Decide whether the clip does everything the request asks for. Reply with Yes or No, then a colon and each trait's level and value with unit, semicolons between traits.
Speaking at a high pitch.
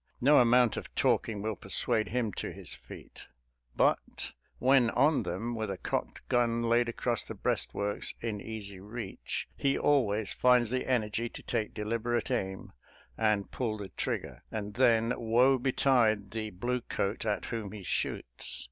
No: low, 115 Hz